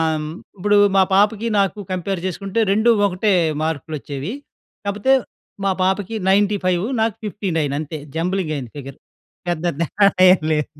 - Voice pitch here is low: No, high, 190 Hz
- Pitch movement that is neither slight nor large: Yes, average, 4.2 semitones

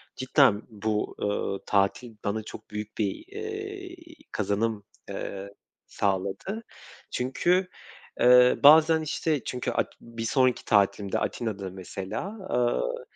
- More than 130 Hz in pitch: No, low, 115 Hz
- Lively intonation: Yes, wide, 7.2 semitones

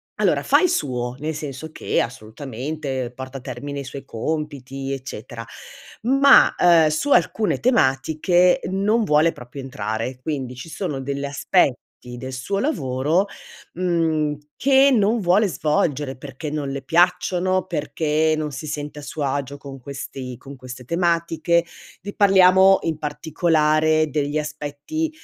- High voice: No, medium, 150 Hz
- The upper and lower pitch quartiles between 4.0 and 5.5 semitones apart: Yes, average, 4.5 semitones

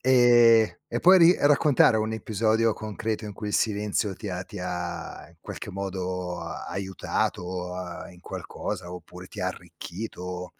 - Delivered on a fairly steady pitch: No, average, 3.7 semitones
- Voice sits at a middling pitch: No, low, 100 Hz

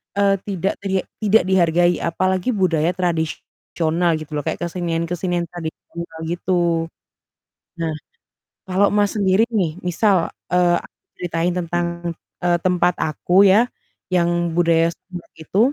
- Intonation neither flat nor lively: No, narrow, 2.0 semitones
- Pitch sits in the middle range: Yes, medium, 175 Hz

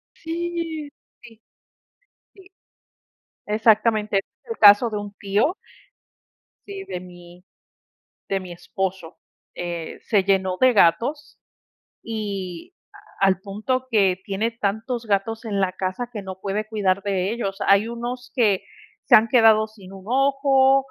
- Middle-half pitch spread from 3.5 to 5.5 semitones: Yes, average, 3.9 semitones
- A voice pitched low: No, high, 210 Hz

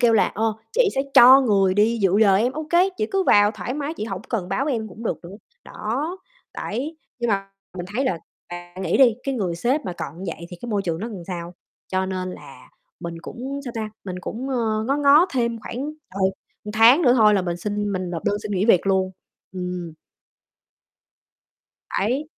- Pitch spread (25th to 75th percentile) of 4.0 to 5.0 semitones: No, wide, 5.6 semitones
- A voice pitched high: Yes, high, 215 Hz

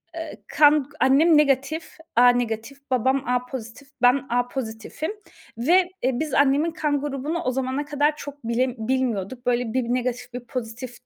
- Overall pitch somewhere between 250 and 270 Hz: Yes, very high, 260 Hz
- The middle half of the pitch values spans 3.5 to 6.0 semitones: No, average, 2.9 semitones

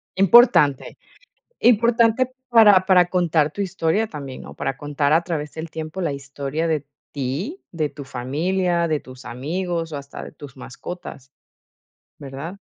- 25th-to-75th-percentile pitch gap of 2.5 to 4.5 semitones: No, average, 5.0 semitones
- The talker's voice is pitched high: No, medium, 160 Hz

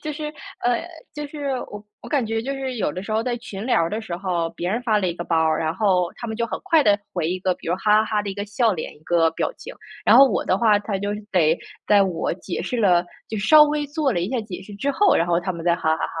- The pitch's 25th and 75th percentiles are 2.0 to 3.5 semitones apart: No, wide, 5.4 semitones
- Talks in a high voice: Yes, high, 205 Hz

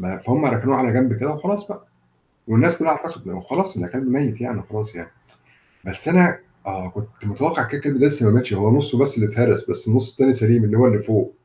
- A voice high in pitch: No, low, 125 Hz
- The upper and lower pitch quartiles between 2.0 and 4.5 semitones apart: No, average, 5.0 semitones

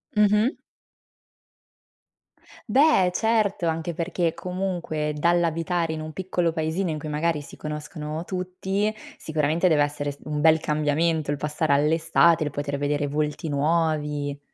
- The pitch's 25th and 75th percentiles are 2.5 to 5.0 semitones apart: Yes, average, 2.8 semitones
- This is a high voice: No, medium, 160 Hz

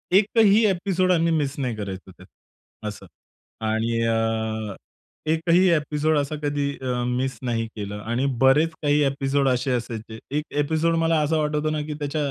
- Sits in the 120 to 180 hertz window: Yes, medium, 140 Hz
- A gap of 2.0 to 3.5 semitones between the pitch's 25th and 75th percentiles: No, wide, 5.4 semitones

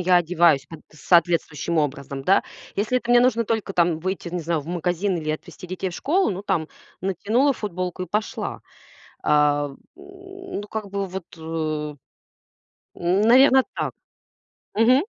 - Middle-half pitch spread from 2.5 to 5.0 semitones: No, wide, 5.4 semitones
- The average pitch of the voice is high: No, medium, 180 Hz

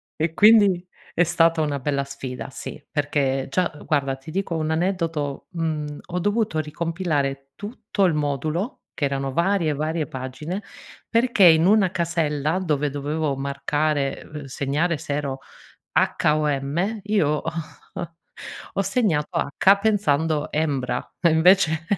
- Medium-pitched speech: Yes, medium, 155 Hz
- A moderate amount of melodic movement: Yes, average, 3.9 semitones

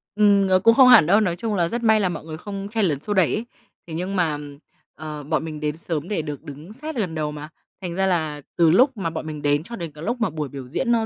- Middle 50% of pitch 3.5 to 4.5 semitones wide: No, wide, 5.4 semitones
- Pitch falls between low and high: Yes, medium, 170 Hz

